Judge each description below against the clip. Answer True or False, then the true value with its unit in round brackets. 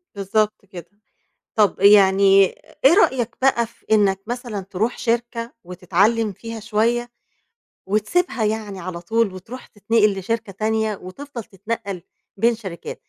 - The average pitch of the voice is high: True (215 Hz)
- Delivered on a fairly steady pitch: False (3.0 semitones)